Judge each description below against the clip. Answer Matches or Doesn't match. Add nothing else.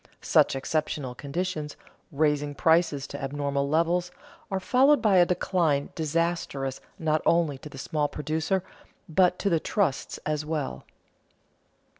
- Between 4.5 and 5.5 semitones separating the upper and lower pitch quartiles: Doesn't match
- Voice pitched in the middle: Matches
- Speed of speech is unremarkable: Doesn't match